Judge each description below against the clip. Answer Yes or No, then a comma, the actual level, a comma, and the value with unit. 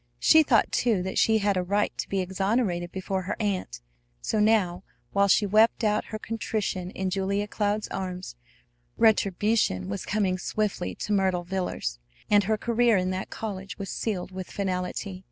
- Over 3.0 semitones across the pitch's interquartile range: No, narrow, 2.6 semitones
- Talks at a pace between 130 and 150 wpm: No, average, 170 wpm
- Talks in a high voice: Yes, high, 195 Hz